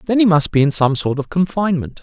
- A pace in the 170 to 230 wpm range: No, fast, 265 wpm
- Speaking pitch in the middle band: Yes, medium, 165 Hz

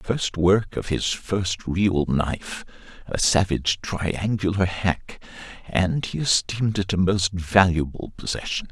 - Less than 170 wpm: Yes, average, 150 wpm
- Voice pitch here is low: Yes, very low, 95 Hz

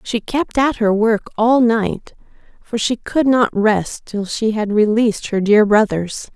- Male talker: No, female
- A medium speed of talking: Yes, average, 180 wpm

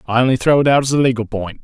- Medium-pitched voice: No, low, 125 Hz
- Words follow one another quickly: Yes, fast, 330 wpm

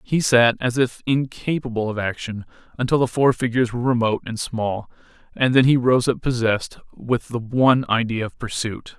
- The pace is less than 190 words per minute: Yes, average, 180 wpm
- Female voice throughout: No, male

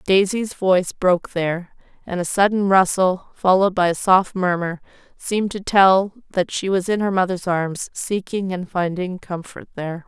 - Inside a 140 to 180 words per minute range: Yes, average, 165 wpm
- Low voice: No, medium, 185 Hz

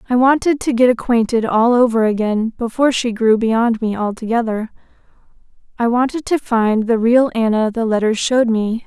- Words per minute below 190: Yes, average, 160 wpm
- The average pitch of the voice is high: Yes, high, 230 Hz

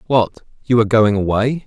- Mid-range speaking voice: No, low, 115 Hz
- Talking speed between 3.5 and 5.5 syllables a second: Yes, 5.2 syllables/s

